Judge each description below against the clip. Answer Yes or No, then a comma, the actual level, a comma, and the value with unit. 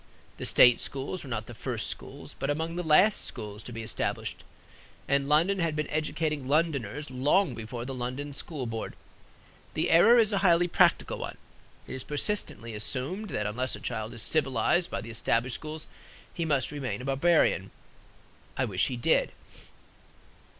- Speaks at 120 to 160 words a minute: No, average, 170 wpm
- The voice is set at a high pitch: No, medium, 140 Hz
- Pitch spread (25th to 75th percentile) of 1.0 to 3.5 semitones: No, average, 5.3 semitones